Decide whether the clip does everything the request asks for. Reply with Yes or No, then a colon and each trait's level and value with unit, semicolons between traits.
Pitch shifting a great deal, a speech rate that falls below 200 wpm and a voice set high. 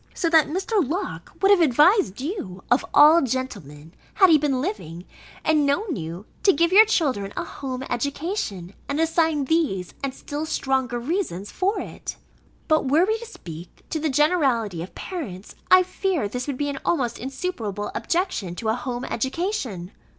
Yes: wide, 7.2 semitones; average, 170 wpm; very high, 280 Hz